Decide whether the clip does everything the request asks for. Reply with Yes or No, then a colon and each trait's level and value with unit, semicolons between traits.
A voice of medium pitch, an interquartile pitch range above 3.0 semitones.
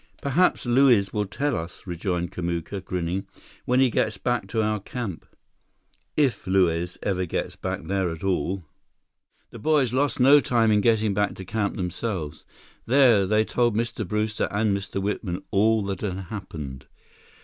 No: low, 105 Hz; average, 4.0 semitones